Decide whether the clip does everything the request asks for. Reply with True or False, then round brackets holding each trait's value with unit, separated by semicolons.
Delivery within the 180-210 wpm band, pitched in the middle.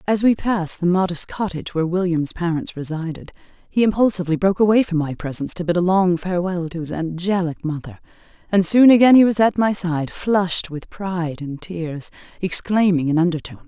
True (185 wpm; 180 Hz)